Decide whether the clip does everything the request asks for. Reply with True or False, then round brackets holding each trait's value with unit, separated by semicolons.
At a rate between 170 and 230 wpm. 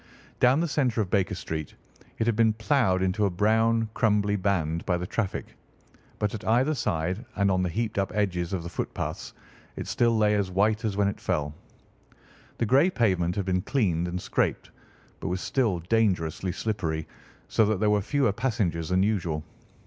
True (185 wpm)